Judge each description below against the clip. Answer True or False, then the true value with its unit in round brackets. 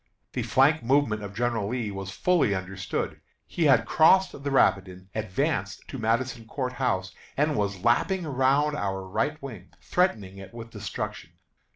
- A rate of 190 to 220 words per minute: False (155 wpm)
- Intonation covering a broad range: True (6.2 semitones)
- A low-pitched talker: True (115 Hz)